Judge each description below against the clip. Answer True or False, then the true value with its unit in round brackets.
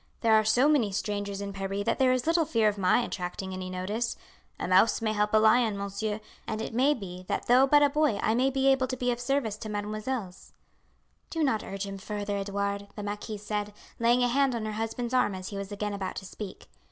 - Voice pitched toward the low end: False (215 Hz)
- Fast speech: True (235 wpm)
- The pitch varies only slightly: False (3.5 semitones)